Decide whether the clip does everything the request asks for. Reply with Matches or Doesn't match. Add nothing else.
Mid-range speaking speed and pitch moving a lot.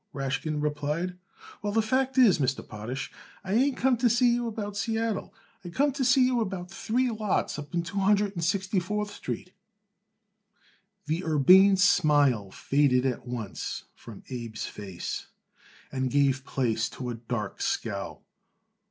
Matches